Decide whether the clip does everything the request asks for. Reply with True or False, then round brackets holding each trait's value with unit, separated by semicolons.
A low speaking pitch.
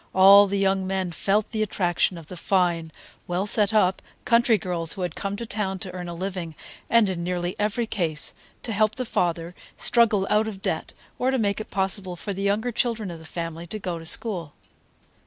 False (190 Hz)